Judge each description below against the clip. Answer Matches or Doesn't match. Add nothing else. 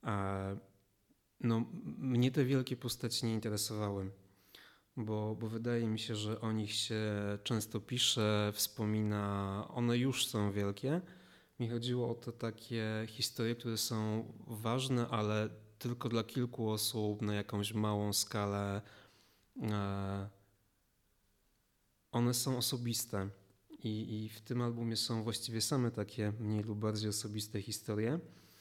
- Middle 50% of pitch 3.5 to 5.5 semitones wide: Doesn't match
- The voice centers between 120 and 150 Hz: Doesn't match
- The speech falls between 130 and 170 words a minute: Doesn't match